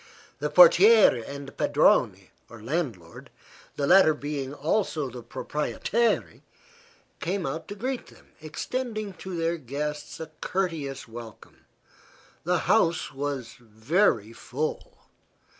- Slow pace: Yes, slow, 115 wpm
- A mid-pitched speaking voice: Yes, medium, 150 Hz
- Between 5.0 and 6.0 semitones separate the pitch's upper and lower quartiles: Yes, wide, 5.4 semitones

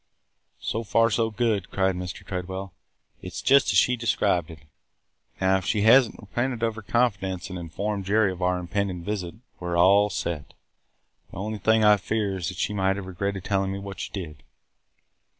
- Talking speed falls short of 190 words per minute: No, average, 195 wpm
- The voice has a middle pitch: No, low, 100 Hz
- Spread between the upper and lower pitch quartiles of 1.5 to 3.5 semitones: Yes, average, 2.8 semitones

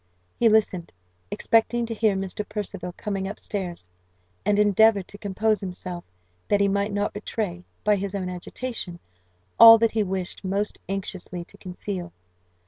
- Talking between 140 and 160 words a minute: Yes, average, 150 wpm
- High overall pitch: Yes, high, 200 Hz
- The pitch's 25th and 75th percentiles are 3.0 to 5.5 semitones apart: No, narrow, 2.4 semitones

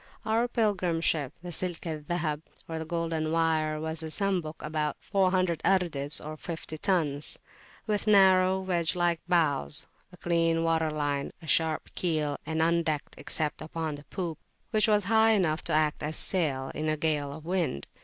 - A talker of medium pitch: Yes, medium, 165 Hz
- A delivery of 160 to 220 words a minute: Yes, average, 175 wpm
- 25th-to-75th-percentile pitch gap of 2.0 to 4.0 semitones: Yes, average, 2.8 semitones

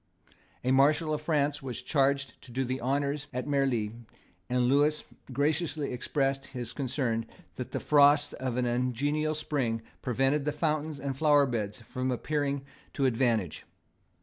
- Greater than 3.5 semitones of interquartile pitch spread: No, average, 2.7 semitones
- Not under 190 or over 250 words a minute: No, average, 150 wpm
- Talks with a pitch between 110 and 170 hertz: Yes, low, 135 Hz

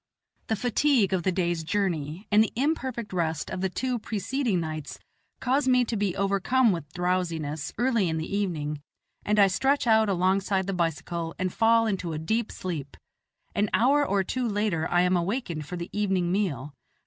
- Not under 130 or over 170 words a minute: No, average, 180 wpm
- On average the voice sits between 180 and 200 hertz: Yes, high, 190 Hz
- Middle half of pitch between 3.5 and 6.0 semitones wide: Yes, average, 4.7 semitones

